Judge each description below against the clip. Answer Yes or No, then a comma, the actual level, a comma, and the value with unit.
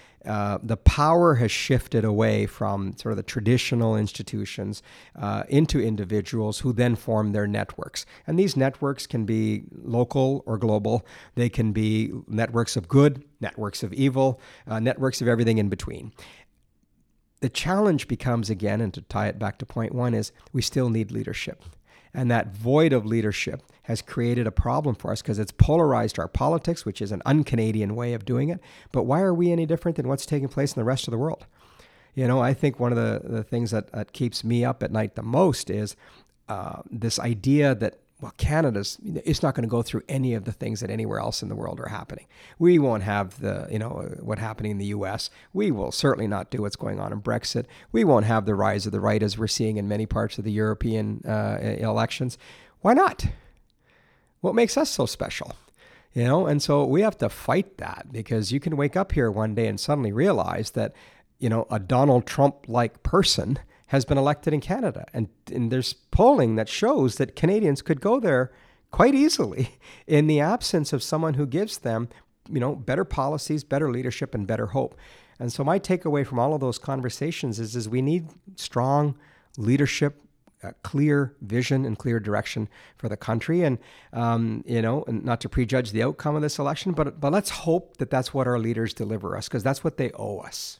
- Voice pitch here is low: Yes, low, 120 Hz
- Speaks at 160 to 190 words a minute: No, average, 200 wpm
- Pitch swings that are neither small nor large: Yes, average, 4.5 semitones